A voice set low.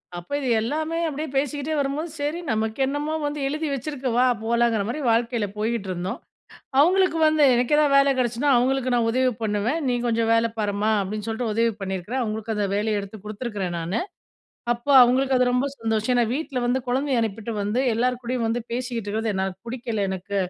No: high, 235 Hz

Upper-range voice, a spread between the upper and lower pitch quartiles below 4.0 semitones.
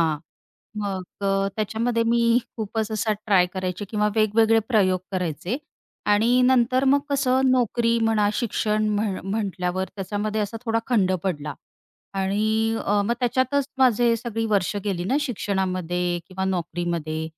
Yes: high, 210 Hz; average, 3.5 semitones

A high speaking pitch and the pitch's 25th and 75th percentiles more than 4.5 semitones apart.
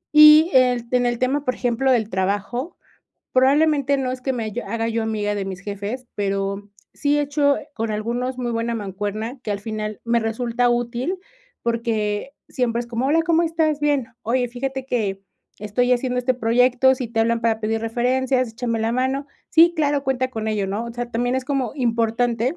No: high, 240 Hz; average, 2.8 semitones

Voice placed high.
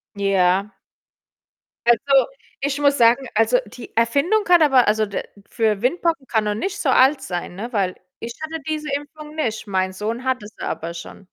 Yes: high, 240 Hz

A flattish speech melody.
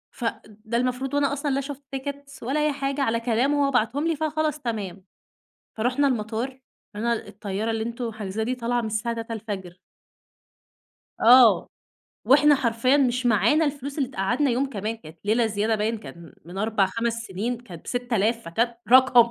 No: average, 3.8 semitones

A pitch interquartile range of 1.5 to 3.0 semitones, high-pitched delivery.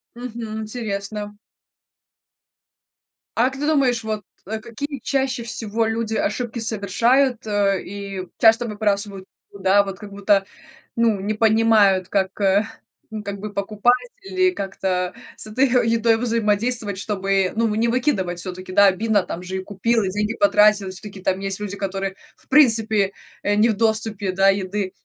Yes: narrow, 2.6 semitones; high, 210 Hz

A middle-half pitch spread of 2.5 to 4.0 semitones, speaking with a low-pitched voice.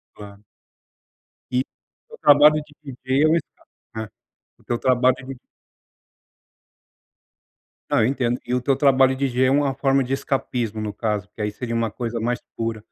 Yes: average, 2.9 semitones; low, 125 Hz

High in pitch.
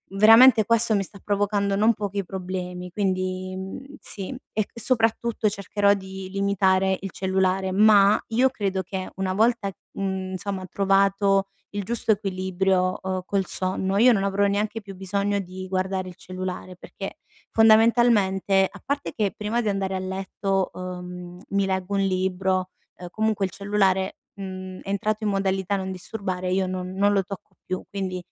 Yes: high, 195 Hz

